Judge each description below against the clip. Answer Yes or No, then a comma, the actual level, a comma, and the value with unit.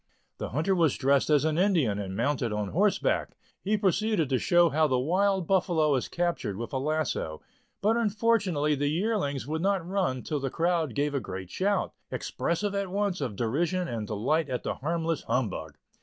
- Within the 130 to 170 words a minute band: No, average, 185 wpm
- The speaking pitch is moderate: Yes, medium, 155 Hz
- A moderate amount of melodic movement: No, wide, 6.3 semitones